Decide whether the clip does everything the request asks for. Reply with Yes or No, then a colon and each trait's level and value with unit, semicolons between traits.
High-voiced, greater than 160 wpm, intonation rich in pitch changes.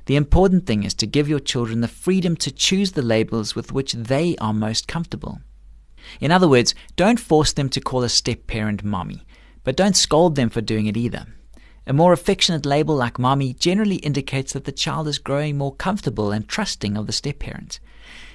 No: low, 135 Hz; average, 200 wpm; wide, 6.4 semitones